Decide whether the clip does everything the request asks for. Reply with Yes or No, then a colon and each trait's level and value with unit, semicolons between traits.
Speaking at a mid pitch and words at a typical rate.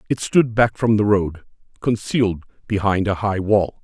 No: low, 105 Hz; average, 170 wpm